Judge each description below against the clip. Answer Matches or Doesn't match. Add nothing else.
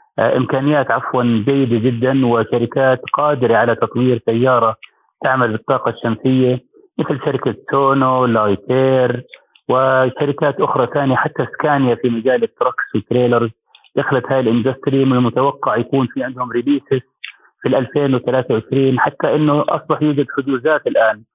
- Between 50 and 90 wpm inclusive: Doesn't match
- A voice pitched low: Matches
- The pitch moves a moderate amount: Doesn't match